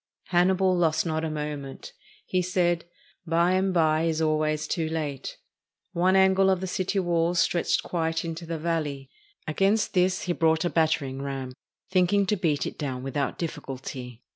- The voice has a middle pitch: Yes, medium, 165 Hz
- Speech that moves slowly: No, average, 165 wpm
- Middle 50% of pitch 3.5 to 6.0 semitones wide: No, average, 3.0 semitones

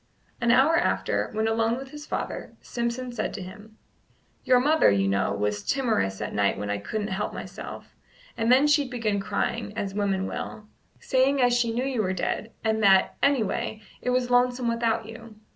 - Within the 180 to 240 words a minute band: Yes, average, 190 wpm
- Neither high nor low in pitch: No, high, 225 Hz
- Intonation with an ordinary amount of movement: Yes, average, 3.7 semitones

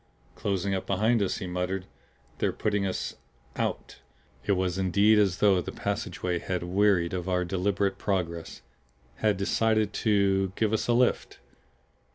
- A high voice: No, very low, 95 Hz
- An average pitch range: No, narrow, 2.3 semitones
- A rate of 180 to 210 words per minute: No, average, 150 wpm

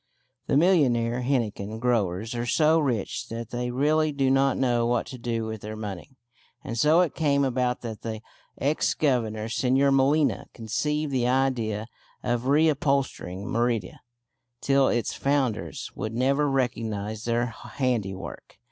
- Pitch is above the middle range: No, low, 125 Hz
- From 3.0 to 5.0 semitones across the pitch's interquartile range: Yes, average, 3.5 semitones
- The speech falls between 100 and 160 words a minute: Yes, average, 140 wpm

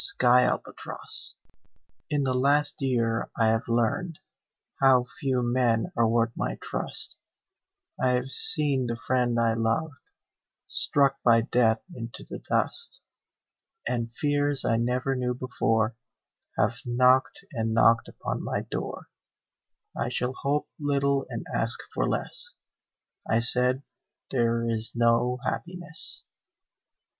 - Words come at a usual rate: No, slow, 125 wpm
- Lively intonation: No, average, 2.8 semitones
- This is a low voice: Yes, low, 125 Hz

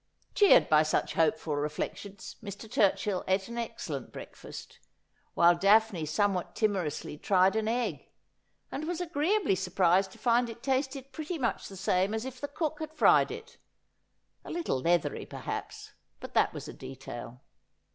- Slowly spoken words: No, average, 155 wpm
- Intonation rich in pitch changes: Yes, wide, 7.2 semitones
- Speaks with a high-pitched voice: Yes, high, 205 Hz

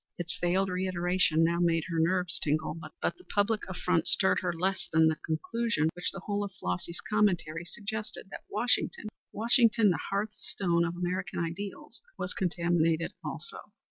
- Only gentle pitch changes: No, average, 3.4 semitones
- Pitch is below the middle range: No, medium, 180 Hz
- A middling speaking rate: Yes, average, 160 wpm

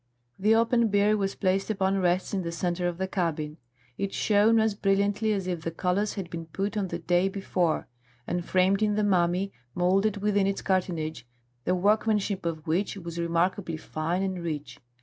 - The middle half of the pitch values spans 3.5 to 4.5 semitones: No, average, 2.9 semitones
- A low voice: No, high, 190 Hz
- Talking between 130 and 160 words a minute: No, average, 185 wpm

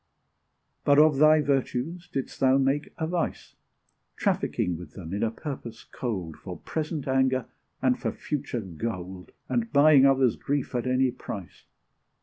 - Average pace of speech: Yes, average, 145 wpm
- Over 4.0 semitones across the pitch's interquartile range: Yes, average, 4.6 semitones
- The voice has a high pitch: No, low, 130 Hz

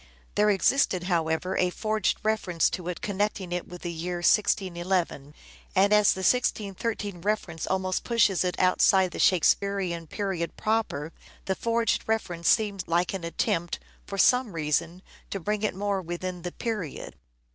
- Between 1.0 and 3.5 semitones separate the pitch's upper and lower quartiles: Yes, average, 3.2 semitones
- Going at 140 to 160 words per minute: Yes, average, 150 wpm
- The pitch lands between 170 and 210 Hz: Yes, medium, 185 Hz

